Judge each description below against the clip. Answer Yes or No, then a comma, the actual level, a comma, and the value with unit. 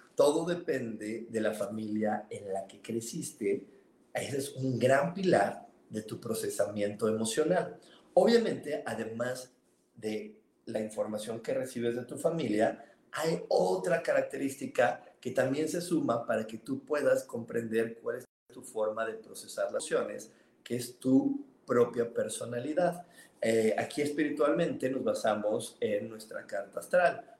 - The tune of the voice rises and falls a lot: Yes, wide, 7.6 semitones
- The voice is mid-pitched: No, low, 125 Hz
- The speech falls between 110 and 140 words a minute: Yes, average, 135 wpm